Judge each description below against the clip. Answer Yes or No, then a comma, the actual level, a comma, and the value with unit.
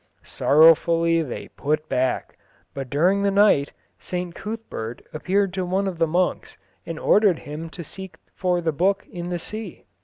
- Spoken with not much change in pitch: No, average, 3.5 semitones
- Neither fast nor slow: Yes, average, 160 wpm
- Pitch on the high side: No, medium, 175 Hz